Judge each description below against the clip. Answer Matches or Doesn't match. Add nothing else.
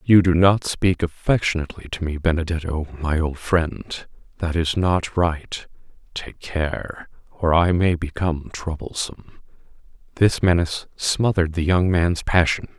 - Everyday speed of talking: Doesn't match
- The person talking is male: Matches